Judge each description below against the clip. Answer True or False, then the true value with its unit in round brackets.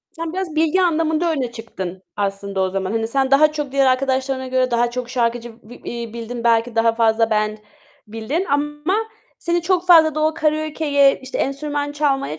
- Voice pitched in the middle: False (265 Hz)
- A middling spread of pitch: True (5.0 semitones)